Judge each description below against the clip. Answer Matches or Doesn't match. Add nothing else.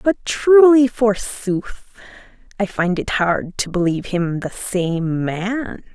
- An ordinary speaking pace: Doesn't match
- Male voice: Doesn't match